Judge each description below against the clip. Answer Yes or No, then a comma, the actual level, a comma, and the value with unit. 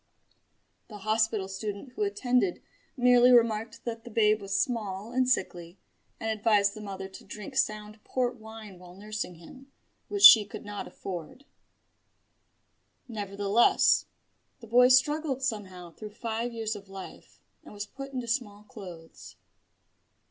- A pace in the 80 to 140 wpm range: Yes, slow, 135 wpm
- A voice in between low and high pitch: No, high, 215 Hz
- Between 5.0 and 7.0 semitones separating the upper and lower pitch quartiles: No, average, 3.4 semitones